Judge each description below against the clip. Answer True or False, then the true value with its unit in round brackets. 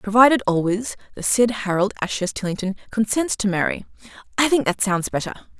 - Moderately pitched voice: False (210 Hz)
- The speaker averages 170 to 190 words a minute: False (160 wpm)